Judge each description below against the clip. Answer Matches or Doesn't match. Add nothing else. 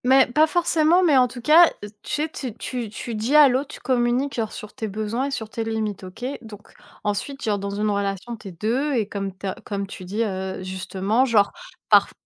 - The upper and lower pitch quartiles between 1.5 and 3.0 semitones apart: Doesn't match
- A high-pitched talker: Matches